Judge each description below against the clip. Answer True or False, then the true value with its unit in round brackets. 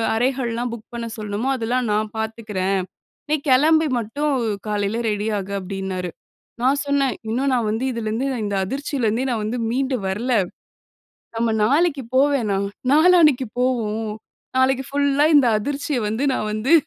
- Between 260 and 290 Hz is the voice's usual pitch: False (235 Hz)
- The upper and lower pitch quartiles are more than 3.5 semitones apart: True (4.2 semitones)